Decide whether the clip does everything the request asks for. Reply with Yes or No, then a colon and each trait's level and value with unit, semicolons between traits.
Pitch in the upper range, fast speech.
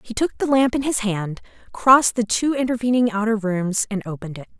Yes: high, 225 Hz; fast, 210 wpm